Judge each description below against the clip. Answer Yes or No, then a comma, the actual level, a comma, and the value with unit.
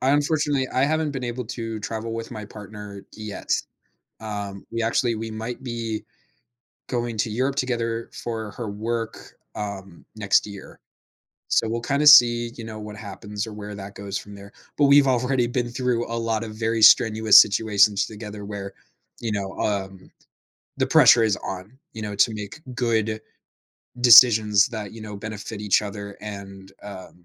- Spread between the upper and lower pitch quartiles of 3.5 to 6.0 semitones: No, narrow, 2.5 semitones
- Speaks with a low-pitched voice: Yes, low, 110 Hz